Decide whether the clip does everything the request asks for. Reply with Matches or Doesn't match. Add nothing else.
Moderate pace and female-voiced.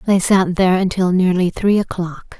Matches